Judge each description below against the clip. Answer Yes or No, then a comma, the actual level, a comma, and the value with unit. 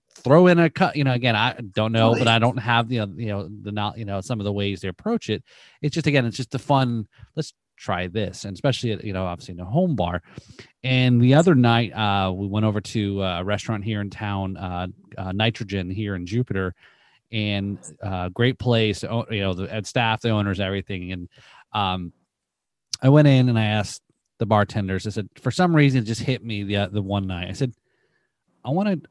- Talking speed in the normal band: No, fast, 220 wpm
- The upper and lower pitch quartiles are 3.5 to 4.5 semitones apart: Yes, average, 3.9 semitones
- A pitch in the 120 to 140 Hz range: No, low, 110 Hz